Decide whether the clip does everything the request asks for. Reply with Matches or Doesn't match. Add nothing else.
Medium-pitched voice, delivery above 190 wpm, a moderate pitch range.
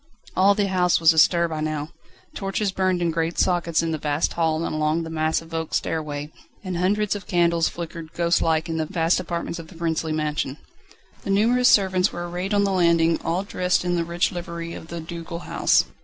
Doesn't match